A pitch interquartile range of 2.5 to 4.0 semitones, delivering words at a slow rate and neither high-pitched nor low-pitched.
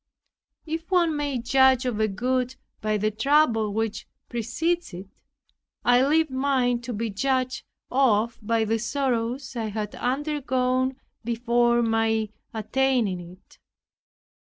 No: average, 3.2 semitones; slow, 125 wpm; high, 245 Hz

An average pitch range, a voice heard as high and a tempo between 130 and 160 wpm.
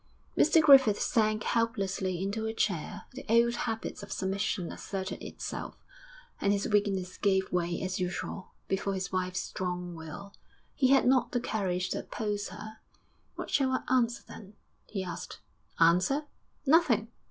Yes: average, 3.6 semitones; high, 200 Hz; average, 150 wpm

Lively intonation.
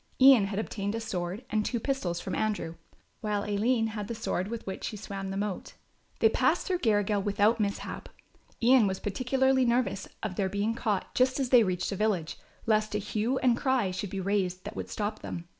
No: average, 3.1 semitones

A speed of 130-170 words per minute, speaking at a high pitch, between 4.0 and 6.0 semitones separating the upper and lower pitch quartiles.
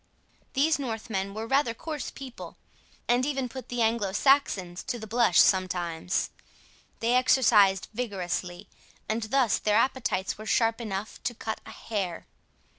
Yes: average, 140 wpm; high, 225 Hz; average, 4.5 semitones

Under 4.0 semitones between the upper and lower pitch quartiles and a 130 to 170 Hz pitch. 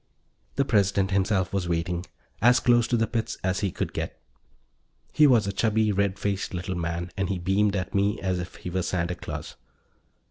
No: average, 2.7 semitones; low, 100 Hz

